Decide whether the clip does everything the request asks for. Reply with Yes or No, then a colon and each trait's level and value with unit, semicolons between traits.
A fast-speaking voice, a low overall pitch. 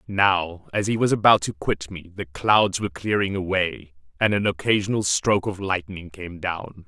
No: average, 185 wpm; very low, 95 Hz